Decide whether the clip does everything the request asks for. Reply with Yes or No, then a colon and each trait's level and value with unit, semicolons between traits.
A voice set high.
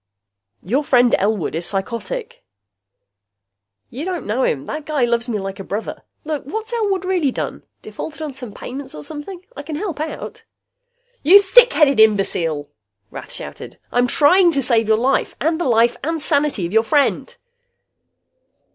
Yes: very high, 275 Hz